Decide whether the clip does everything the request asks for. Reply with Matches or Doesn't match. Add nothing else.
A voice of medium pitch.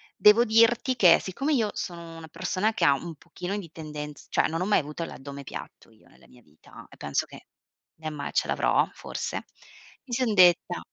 Matches